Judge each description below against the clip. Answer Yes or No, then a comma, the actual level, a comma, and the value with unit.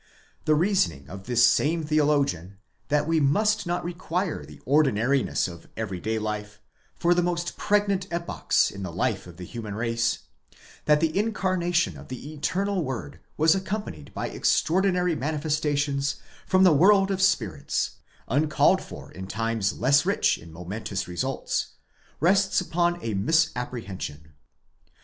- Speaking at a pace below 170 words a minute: Yes, average, 140 wpm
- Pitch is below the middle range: No, medium, 145 Hz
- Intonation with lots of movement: Yes, wide, 8.4 semitones